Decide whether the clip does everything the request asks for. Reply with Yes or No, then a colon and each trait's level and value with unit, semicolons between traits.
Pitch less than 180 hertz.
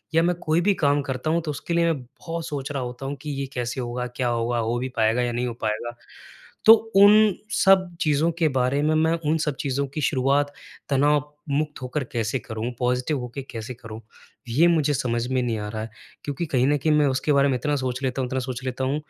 Yes: low, 135 Hz